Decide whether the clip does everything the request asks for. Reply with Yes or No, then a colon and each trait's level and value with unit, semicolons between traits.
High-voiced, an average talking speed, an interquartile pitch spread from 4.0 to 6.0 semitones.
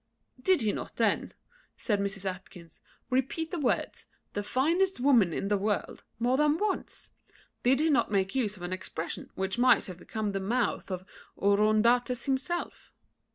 Yes: high, 220 Hz; average, 160 wpm; average, 5.3 semitones